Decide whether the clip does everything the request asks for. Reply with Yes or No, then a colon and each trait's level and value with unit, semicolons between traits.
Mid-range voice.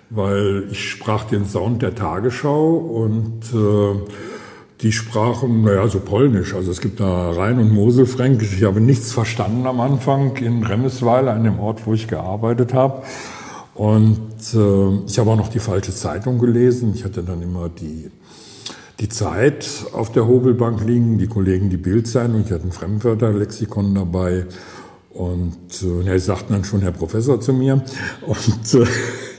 No: low, 110 Hz